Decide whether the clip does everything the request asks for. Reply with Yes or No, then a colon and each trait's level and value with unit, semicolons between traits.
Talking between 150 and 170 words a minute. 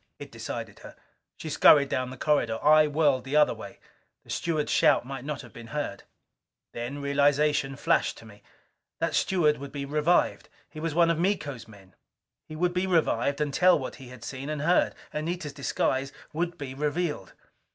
No: average, 185 wpm